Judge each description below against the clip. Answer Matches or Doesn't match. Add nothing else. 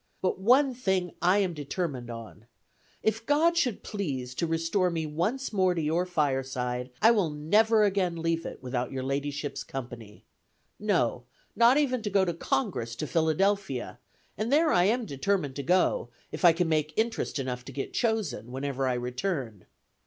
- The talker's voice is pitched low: Doesn't match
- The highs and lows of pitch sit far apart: Matches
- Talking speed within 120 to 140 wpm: Doesn't match